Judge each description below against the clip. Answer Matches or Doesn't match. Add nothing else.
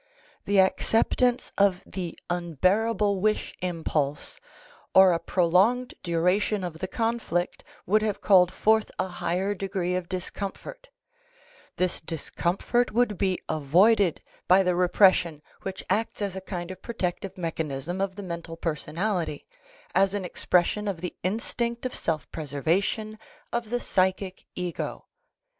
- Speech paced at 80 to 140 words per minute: Matches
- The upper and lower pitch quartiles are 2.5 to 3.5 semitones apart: Matches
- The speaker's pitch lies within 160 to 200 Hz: Matches